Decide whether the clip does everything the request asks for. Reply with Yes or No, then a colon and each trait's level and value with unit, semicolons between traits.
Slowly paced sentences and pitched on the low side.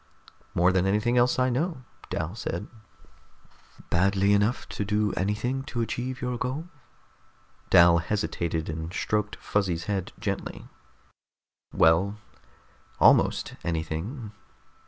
Yes: slow, 110 wpm; low, 105 Hz